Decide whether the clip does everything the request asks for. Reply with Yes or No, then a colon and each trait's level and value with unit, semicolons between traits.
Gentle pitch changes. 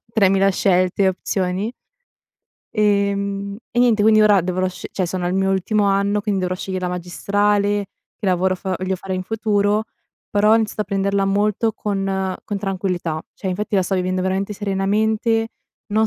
Yes: narrow, 1.8 semitones